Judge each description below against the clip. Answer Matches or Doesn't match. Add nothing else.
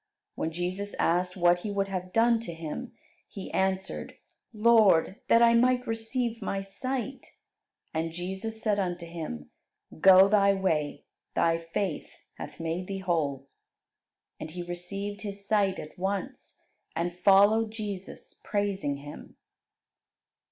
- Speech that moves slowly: Matches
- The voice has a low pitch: Doesn't match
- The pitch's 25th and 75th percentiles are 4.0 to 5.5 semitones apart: Doesn't match